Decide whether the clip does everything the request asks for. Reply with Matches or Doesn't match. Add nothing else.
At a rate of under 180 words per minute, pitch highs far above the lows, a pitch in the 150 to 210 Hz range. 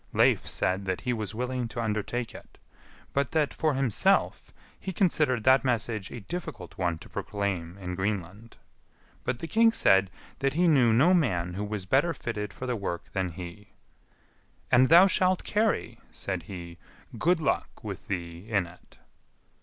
Doesn't match